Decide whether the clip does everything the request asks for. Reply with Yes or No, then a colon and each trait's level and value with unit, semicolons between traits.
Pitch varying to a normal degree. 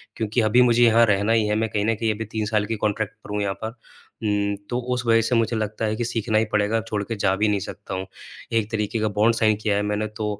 No: narrow, 1.6 semitones